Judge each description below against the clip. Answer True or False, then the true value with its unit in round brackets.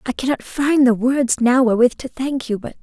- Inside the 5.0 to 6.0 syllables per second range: True (5.2 syllables/s)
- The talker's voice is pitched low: False (255 Hz)